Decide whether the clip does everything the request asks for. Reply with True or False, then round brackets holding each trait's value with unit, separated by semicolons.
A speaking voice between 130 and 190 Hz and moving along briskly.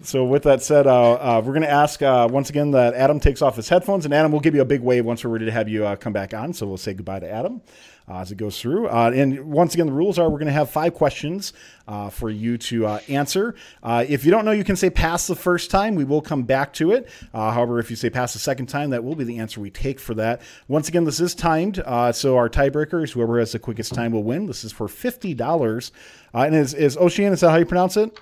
True (135 Hz; 285 wpm)